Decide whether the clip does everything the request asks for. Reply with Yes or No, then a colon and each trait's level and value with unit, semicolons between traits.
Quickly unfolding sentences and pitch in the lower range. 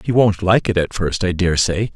Yes: fast, 245 wpm; very low, 95 Hz